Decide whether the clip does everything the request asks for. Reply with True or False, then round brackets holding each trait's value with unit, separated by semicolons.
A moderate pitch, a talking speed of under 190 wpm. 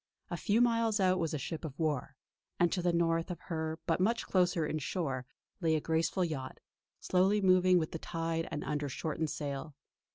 False (165 Hz; 195 wpm)